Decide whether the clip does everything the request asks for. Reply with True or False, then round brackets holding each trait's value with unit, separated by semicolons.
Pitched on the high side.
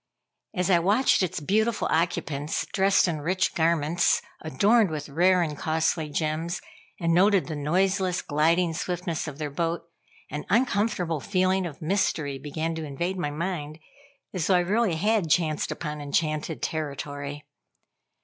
False (165 Hz)